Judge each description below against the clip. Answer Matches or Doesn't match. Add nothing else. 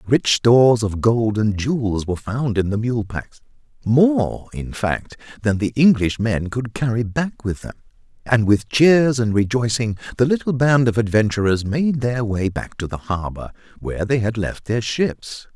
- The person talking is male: Matches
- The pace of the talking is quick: Doesn't match